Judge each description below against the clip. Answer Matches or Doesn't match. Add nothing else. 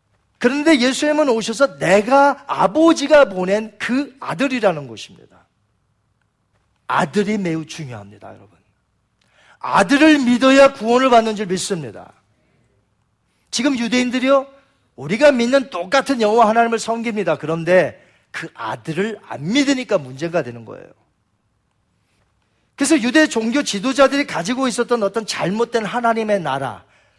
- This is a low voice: Doesn't match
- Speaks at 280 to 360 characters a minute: Matches